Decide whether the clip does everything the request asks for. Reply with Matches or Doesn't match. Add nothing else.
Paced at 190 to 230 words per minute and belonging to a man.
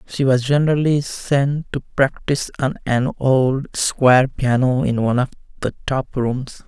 Doesn't match